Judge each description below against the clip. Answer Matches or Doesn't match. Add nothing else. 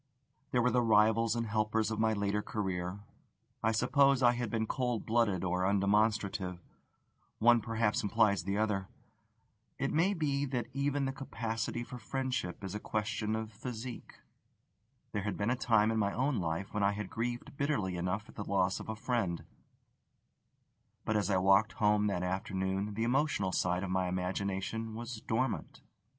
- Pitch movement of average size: Matches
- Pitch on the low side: Matches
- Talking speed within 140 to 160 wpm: Doesn't match